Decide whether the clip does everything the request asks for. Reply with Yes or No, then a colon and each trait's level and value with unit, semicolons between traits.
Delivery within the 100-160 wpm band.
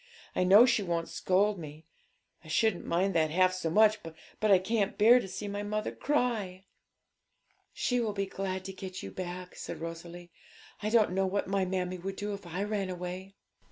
No: average, 195 wpm